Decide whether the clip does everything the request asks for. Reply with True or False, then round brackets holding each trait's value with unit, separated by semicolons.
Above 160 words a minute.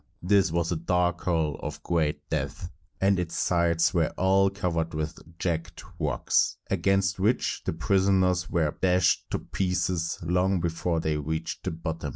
False (155 wpm)